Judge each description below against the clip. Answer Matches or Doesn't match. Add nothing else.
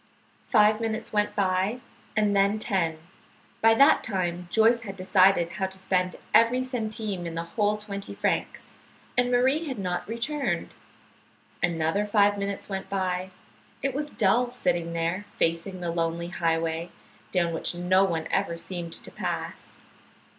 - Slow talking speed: Doesn't match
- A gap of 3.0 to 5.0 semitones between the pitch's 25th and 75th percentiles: Matches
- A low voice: Doesn't match